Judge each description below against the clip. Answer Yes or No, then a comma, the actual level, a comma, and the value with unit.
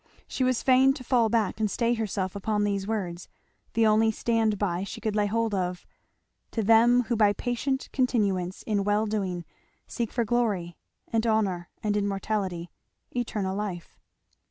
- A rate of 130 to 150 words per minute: No, average, 160 wpm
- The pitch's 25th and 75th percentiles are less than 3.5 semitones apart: Yes, average, 2.8 semitones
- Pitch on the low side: No, high, 215 Hz